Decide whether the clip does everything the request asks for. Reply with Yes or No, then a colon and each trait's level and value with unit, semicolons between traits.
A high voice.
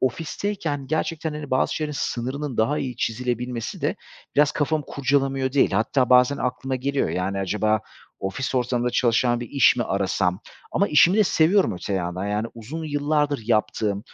No: low, 130 Hz